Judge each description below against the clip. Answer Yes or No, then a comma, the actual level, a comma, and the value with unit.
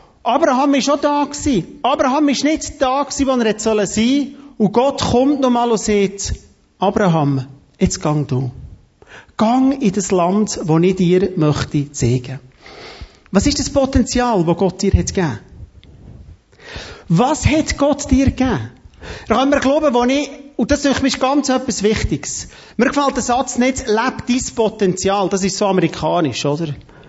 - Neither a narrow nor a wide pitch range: No, wide, 7.2 semitones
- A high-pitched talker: Yes, high, 225 Hz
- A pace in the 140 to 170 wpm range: Yes, average, 165 wpm